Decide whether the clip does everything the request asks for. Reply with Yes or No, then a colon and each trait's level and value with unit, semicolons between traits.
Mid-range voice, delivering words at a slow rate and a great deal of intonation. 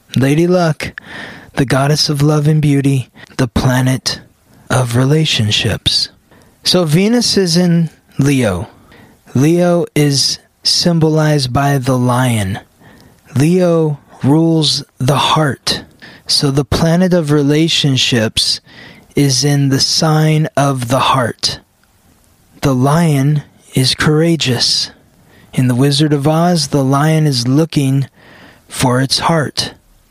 No: medium, 145 Hz; slow, 110 wpm; average, 3.3 semitones